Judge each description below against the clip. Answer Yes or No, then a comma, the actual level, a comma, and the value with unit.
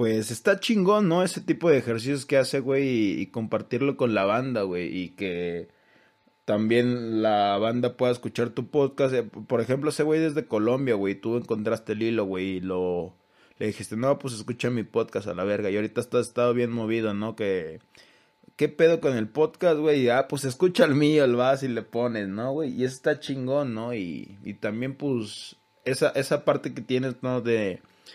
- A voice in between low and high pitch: No, low, 120 Hz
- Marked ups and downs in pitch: No, average, 3.9 semitones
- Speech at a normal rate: No, fast, 195 wpm